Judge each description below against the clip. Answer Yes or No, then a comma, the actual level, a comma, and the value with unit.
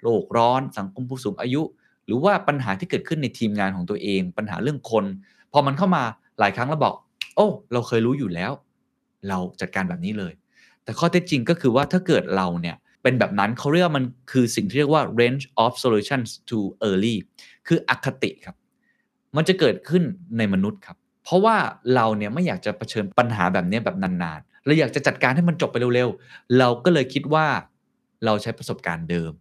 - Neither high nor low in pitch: No, low, 125 Hz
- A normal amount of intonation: No, wide, 7.0 semitones